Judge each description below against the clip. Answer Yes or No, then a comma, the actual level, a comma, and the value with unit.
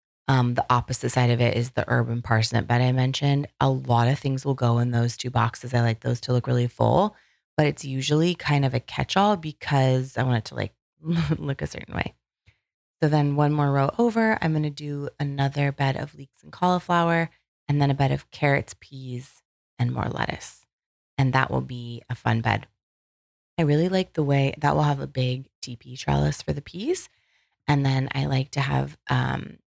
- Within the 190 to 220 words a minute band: Yes, fast, 205 wpm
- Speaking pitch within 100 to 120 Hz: No, low, 135 Hz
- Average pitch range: Yes, average, 3.4 semitones